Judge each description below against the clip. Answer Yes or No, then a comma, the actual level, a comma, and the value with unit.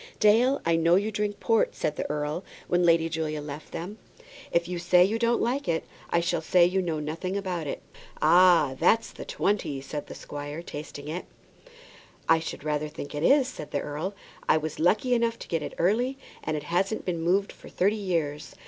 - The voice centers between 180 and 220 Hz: No, medium, 170 Hz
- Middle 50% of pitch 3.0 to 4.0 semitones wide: No, average, 4.7 semitones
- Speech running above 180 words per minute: Yes, average, 200 wpm